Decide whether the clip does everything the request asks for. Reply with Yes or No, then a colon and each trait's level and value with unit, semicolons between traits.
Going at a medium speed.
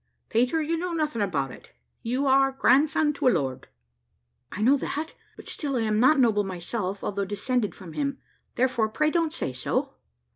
Yes: average, 180 wpm